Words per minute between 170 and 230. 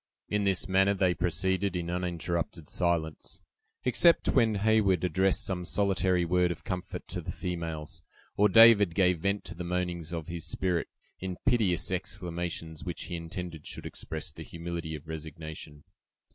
No: average, 155 wpm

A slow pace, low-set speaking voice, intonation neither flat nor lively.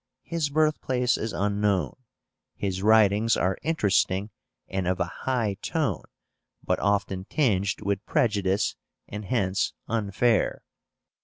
Yes: slow, 110 wpm; low, 105 Hz; average, 3.6 semitones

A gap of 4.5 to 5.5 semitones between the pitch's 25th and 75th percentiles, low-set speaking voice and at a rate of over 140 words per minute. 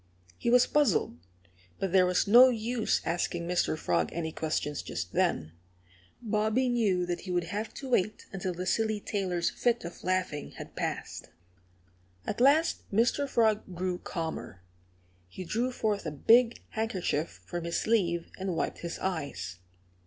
No: average, 4.8 semitones; medium, 185 Hz; average, 155 wpm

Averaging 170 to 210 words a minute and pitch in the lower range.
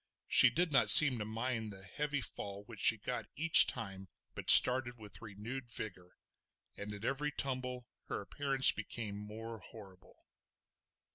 No: average, 150 wpm; low, 115 Hz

